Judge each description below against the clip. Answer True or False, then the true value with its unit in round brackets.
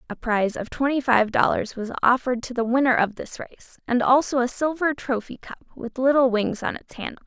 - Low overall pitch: False (250 Hz)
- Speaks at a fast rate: True (215 wpm)